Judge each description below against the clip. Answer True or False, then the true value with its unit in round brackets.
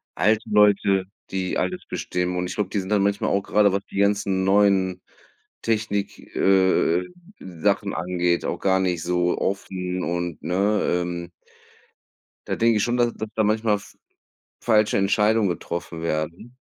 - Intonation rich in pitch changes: False (2.7 semitones)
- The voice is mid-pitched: False (95 Hz)